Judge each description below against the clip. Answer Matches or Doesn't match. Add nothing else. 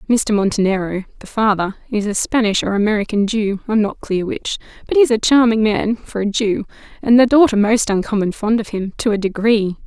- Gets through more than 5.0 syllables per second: Matches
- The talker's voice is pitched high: Matches